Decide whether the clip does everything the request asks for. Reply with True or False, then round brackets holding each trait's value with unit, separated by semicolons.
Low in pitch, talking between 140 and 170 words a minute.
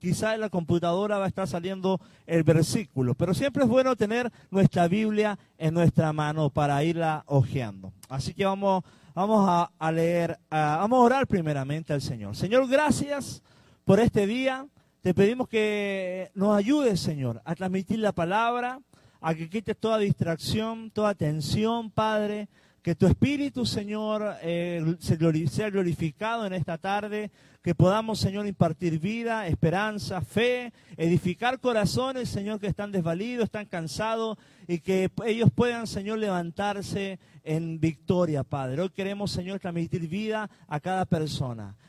False (190 Hz; 145 wpm)